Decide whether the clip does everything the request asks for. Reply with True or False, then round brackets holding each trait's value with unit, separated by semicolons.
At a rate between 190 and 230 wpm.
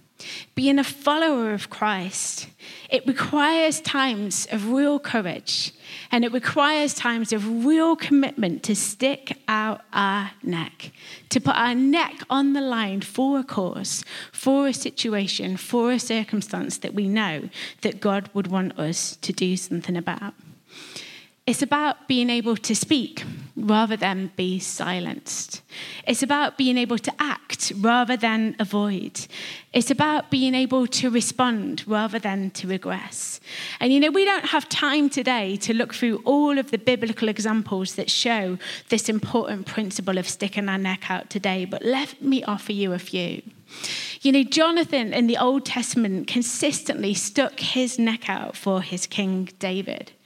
False (155 wpm)